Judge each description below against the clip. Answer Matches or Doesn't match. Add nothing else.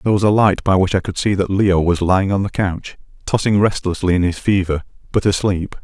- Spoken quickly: Matches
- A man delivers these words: Matches